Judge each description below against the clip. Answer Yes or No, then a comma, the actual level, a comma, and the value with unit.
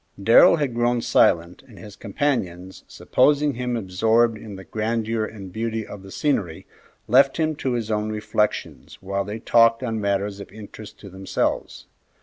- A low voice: Yes, low, 110 Hz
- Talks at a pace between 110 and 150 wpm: No, average, 160 wpm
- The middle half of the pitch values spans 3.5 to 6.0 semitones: No, average, 3.1 semitones